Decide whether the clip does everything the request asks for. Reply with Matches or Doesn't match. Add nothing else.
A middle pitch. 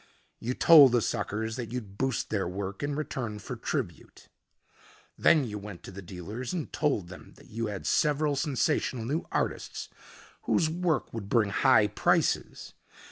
Doesn't match